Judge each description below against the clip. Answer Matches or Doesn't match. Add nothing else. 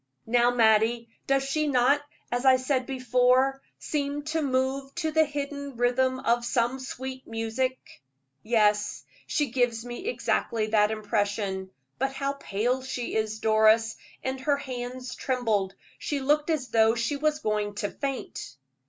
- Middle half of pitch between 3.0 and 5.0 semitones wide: Matches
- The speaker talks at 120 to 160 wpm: Matches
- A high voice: Matches